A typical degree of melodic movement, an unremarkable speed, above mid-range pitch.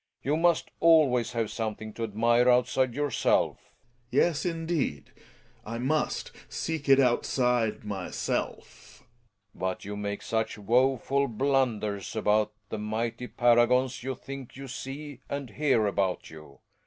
No: average, 4.2 semitones; average, 150 wpm; low, 120 Hz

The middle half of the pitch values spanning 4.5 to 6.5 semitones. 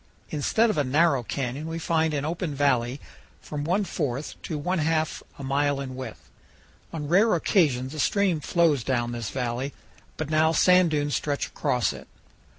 No: average, 3.5 semitones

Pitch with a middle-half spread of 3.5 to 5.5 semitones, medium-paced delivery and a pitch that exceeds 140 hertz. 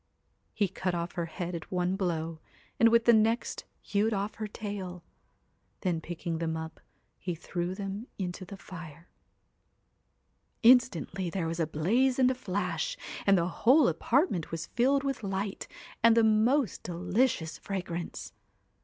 Yes: average, 4.8 semitones; average, 150 wpm; high, 190 Hz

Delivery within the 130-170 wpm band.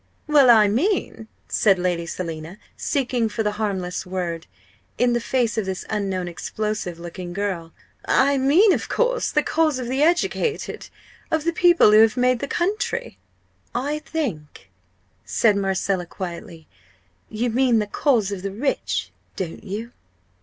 Yes: average, 155 wpm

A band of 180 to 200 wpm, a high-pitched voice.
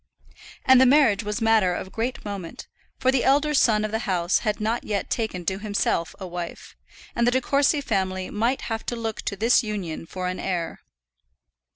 Yes: average, 195 wpm; high, 215 Hz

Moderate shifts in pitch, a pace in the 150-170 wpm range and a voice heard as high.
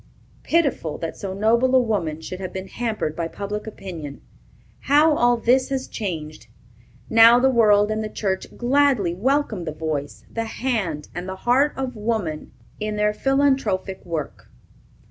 No: wide, 5.8 semitones; average, 155 wpm; high, 210 Hz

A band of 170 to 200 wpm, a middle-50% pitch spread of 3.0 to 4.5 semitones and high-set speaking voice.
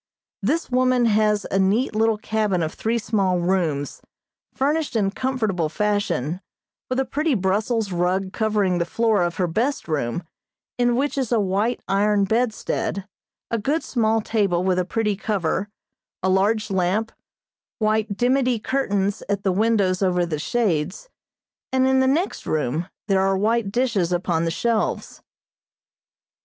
No: average, 150 wpm; average, 3.9 semitones; high, 210 Hz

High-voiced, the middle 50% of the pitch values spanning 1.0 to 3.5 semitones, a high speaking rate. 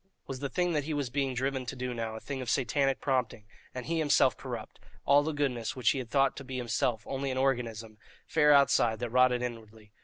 No: low, 130 Hz; average, 2.8 semitones; fast, 225 wpm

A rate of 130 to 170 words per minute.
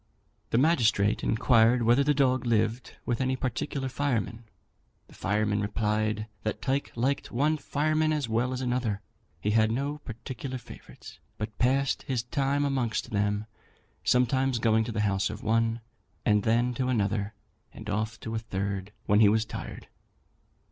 Yes: average, 155 wpm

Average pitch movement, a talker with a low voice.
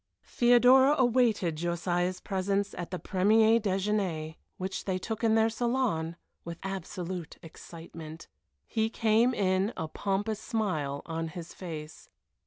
No: average, 4.7 semitones; high, 190 Hz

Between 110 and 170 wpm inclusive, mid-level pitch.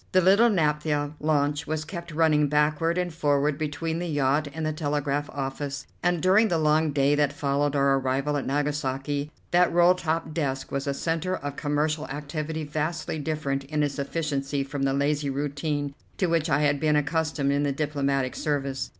No: average, 180 wpm; medium, 150 Hz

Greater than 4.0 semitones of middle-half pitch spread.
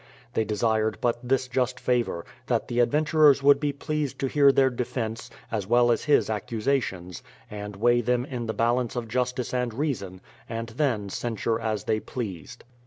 No: average, 3.0 semitones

